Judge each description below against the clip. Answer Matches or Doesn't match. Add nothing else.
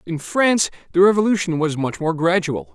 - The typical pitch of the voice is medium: Matches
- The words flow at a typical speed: Matches